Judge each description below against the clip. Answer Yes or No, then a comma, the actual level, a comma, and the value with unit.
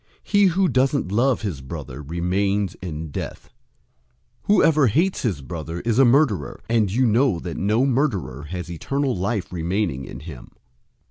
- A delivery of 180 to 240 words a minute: No, average, 155 wpm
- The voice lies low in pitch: Yes, low, 100 Hz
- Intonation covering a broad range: Yes, wide, 7.6 semitones